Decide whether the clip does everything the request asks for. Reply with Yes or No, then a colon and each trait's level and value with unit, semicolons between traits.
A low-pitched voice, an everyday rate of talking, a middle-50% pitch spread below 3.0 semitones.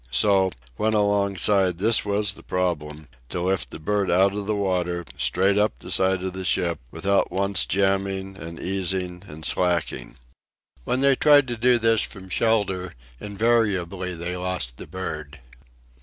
Yes: very low, 95 Hz; average, 155 wpm; narrow, 2.5 semitones